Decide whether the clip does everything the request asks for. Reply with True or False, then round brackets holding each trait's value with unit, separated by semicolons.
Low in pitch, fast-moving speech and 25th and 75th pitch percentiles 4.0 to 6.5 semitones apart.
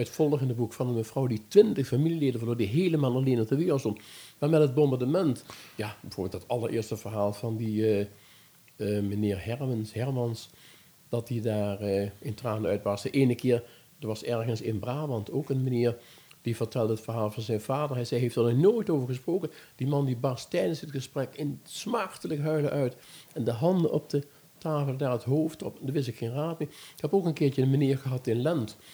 True (125 Hz; 215 wpm; 4.5 semitones)